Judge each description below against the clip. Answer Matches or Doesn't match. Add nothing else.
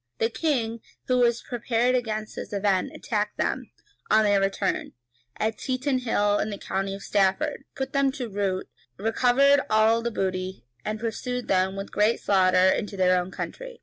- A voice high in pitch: Matches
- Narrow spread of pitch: Doesn't match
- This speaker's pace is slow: Doesn't match